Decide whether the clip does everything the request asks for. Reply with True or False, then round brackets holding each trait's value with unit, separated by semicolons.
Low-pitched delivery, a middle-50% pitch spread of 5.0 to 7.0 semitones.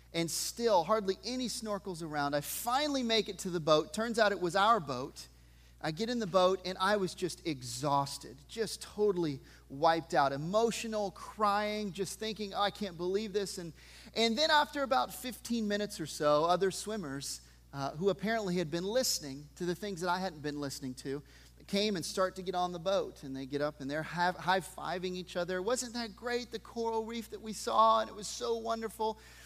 False (190 Hz; 5.4 semitones)